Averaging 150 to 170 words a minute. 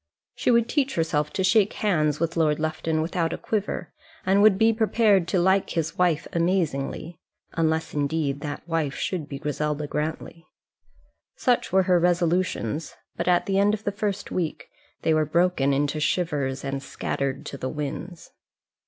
Yes: average, 165 wpm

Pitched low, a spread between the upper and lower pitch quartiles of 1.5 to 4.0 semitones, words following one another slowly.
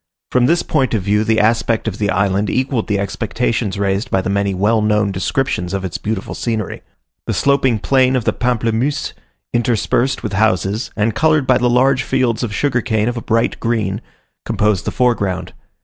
No: low, 110 Hz; average, 3.7 semitones; average, 185 wpm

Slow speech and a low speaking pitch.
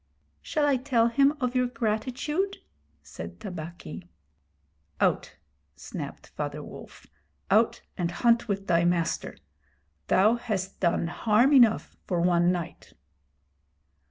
No: slow, 115 wpm; high, 215 Hz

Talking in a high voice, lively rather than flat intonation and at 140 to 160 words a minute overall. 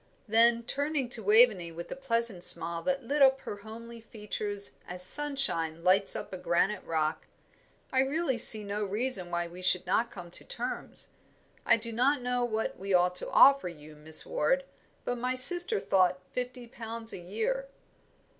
No: high, 220 Hz; wide, 5.9 semitones; average, 175 wpm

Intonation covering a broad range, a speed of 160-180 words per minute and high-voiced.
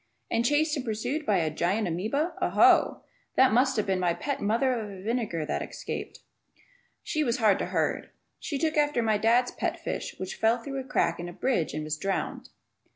No: wide, 5.9 semitones; fast, 205 wpm; high, 225 Hz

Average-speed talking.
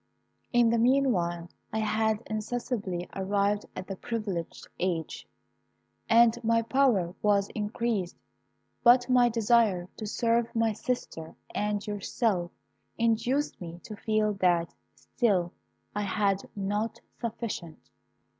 No: slow, 115 wpm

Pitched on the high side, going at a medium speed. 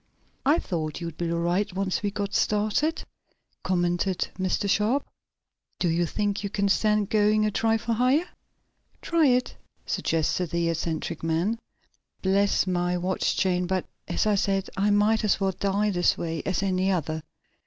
Yes: high, 195 Hz; average, 160 wpm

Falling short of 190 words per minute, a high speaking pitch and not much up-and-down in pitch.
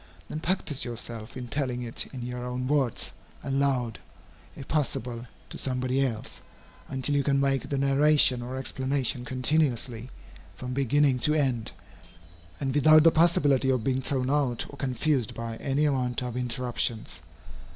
No: average, 150 wpm; low, 130 Hz; narrow, 2.3 semitones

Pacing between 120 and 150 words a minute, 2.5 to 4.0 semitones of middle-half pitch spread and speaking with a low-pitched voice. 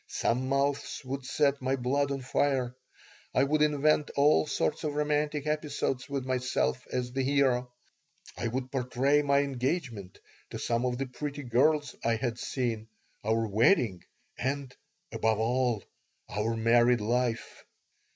Yes: average, 140 wpm; average, 2.8 semitones; low, 130 Hz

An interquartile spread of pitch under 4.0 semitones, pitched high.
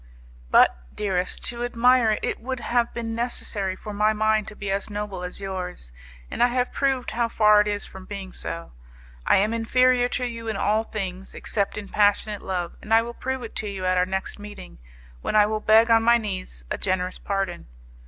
Yes: average, 3.2 semitones; high, 210 Hz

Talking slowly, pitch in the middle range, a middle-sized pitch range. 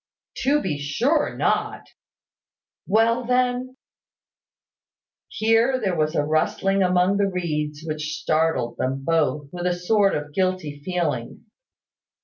No: slow, 125 wpm; medium, 180 Hz; wide, 6.4 semitones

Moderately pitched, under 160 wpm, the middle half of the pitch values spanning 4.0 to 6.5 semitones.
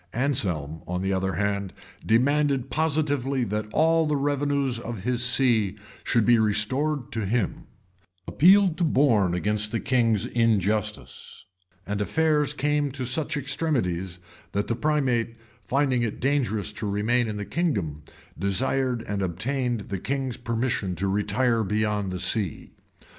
No: low, 115 Hz; average, 140 wpm; average, 5.3 semitones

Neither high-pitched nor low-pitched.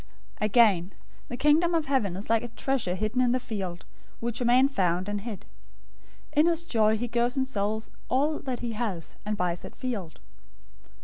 No: high, 230 Hz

